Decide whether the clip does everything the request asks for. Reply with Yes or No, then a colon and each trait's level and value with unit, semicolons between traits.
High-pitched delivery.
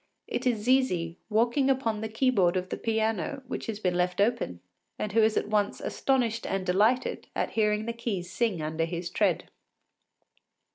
Yes: high, 215 Hz